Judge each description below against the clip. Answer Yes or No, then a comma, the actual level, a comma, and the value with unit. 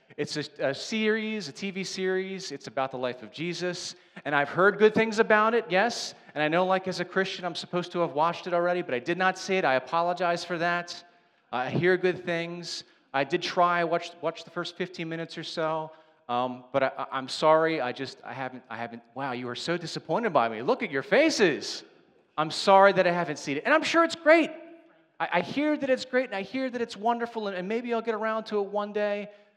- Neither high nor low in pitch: Yes, medium, 175 Hz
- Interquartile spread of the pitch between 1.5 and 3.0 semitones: No, average, 4.7 semitones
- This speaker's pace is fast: Yes, fast, 235 wpm